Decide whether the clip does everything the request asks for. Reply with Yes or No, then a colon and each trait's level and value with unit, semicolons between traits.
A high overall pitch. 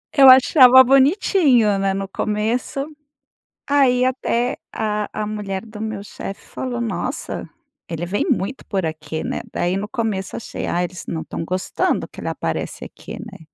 Yes: high, 215 Hz